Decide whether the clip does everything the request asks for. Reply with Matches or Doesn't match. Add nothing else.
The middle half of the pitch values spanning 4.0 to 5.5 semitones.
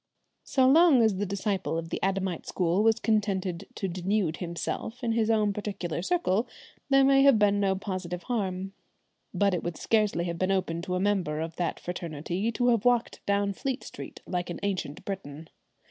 Doesn't match